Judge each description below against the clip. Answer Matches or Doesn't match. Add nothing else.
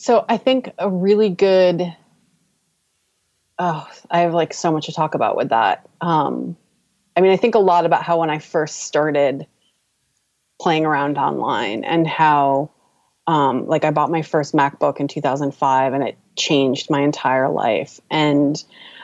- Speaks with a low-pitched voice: Doesn't match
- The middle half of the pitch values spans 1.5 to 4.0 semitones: Matches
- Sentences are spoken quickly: Doesn't match